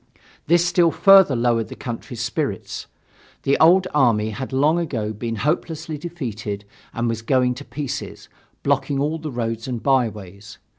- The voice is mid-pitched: No, low, 130 Hz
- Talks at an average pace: Yes, average, 150 wpm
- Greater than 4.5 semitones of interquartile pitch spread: Yes, average, 5.1 semitones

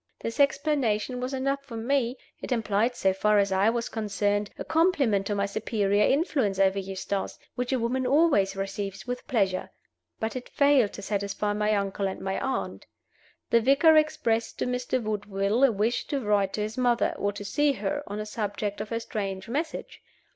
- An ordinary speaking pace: Yes, average, 185 wpm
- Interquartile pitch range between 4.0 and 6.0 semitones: Yes, average, 4.3 semitones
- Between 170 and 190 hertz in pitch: No, high, 220 Hz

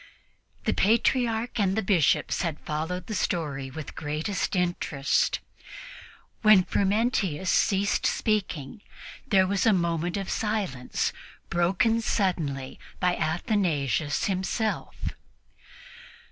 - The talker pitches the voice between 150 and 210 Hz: Yes, medium, 185 Hz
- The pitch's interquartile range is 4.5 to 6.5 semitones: Yes, average, 4.9 semitones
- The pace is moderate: No, slow, 105 wpm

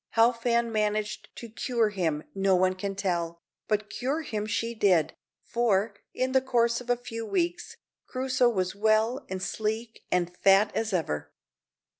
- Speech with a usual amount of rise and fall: Yes, average, 3.6 semitones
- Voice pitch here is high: Yes, high, 215 Hz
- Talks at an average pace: Yes, average, 165 wpm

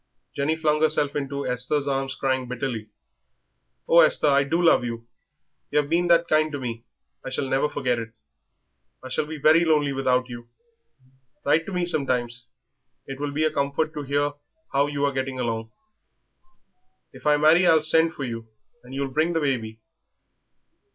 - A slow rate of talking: No, average, 175 wpm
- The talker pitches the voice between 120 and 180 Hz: Yes, medium, 140 Hz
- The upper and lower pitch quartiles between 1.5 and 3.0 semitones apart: No, average, 3.4 semitones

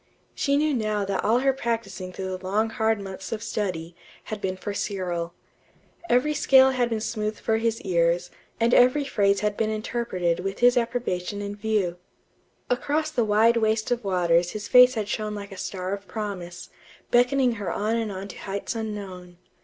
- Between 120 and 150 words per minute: No, average, 185 wpm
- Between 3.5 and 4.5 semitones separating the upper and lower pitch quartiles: Yes, average, 3.8 semitones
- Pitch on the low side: No, high, 210 Hz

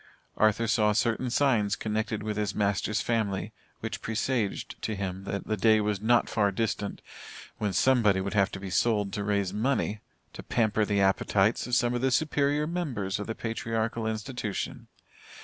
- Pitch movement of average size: No, narrow, 2.3 semitones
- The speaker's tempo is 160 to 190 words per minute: Yes, average, 170 wpm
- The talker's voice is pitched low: Yes, low, 110 Hz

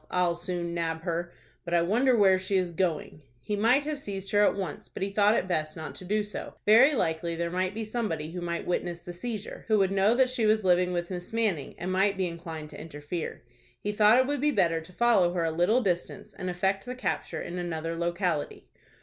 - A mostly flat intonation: No, average, 3.6 semitones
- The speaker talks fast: Yes, fast, 230 wpm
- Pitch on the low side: No, medium, 185 Hz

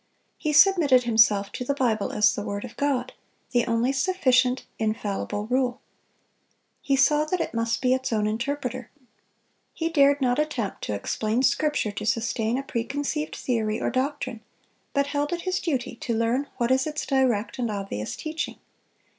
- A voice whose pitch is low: No, very high, 250 Hz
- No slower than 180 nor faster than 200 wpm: No, average, 165 wpm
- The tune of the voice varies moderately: Yes, average, 4.1 semitones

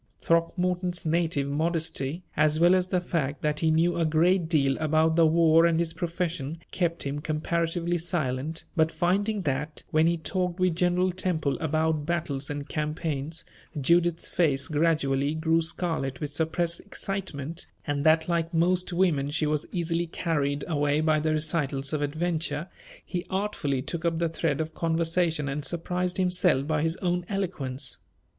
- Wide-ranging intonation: No, narrow, 2.5 semitones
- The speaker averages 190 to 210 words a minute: No, average, 160 wpm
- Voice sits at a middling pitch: Yes, medium, 160 Hz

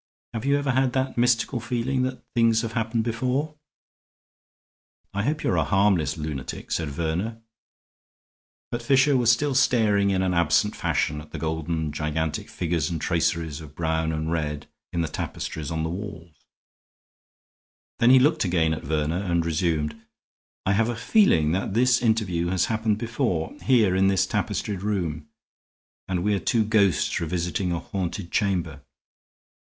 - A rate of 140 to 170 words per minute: Yes, average, 160 wpm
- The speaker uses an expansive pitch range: Yes, wide, 6.3 semitones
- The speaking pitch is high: No, very low, 95 Hz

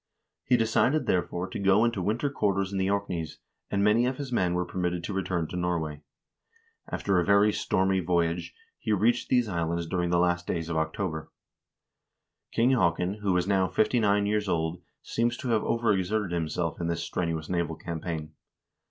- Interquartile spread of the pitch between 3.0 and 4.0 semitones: Yes, average, 3.6 semitones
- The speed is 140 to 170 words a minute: No, average, 180 wpm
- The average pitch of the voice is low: Yes, very low, 95 Hz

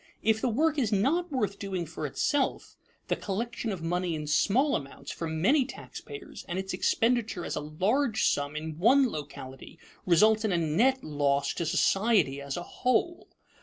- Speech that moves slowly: No, average, 170 wpm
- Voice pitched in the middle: No, high, 195 Hz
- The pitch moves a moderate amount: No, wide, 7.6 semitones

